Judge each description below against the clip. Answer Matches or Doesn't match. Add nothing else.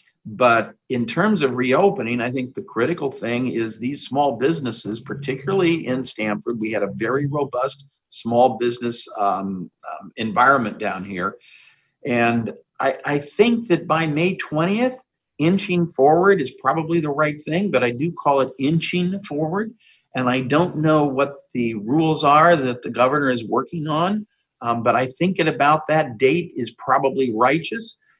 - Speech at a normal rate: Matches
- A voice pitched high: Doesn't match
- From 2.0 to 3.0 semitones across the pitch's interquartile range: Doesn't match